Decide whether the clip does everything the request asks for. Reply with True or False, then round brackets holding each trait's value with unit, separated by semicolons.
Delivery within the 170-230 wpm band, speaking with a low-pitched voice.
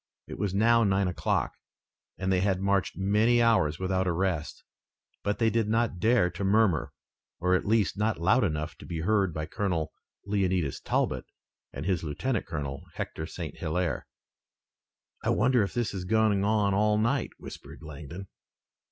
False (160 wpm; 95 Hz)